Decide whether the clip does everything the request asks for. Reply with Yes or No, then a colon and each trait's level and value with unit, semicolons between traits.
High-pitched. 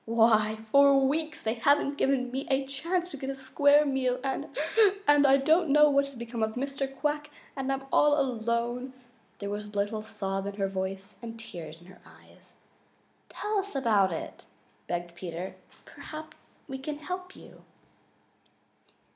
Yes: very high, 265 Hz